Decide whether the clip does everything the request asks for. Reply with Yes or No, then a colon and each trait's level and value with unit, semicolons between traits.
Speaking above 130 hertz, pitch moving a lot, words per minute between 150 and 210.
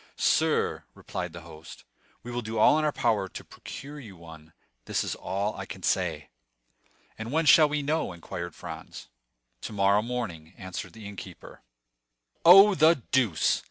No: low, 105 Hz; wide, 8.3 semitones; average, 155 wpm